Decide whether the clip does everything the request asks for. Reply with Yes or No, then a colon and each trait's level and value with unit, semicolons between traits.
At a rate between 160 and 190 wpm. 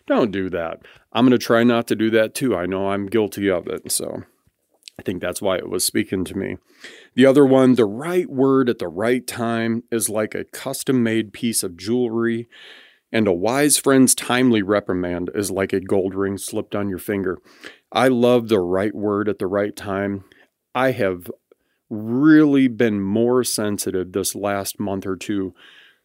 Yes: average, 185 wpm